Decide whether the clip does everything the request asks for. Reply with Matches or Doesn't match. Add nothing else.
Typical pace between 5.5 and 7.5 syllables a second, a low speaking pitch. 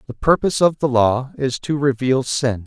Doesn't match